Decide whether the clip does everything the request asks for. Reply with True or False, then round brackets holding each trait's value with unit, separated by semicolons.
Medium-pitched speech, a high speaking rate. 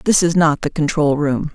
True (155 Hz; 235 wpm)